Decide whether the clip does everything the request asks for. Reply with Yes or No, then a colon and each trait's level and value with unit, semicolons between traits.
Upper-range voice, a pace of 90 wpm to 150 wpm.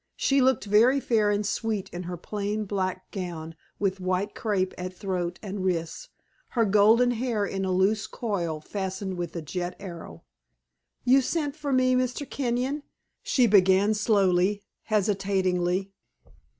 Yes: high, 200 Hz; average, 145 wpm